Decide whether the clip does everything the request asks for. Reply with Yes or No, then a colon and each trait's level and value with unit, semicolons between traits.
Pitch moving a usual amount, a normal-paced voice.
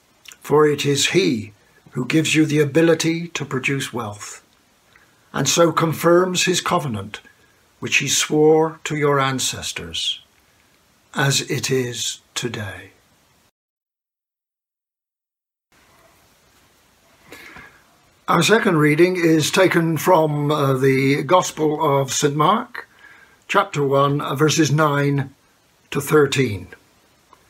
No: average, 3.3 semitones; slow, 100 wpm